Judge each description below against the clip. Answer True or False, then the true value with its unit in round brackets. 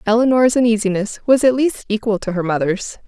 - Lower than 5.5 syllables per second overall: False (5.8 syllables/s)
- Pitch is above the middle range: True (220 Hz)